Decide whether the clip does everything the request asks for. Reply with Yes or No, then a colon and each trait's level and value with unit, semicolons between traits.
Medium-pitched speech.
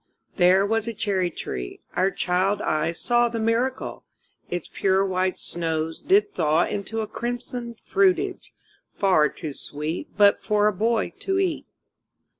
No: high, 200 Hz